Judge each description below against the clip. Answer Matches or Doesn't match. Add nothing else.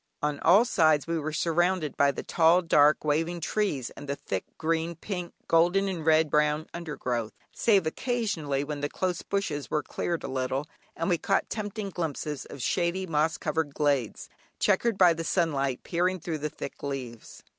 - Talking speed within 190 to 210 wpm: Doesn't match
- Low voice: Doesn't match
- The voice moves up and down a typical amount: Matches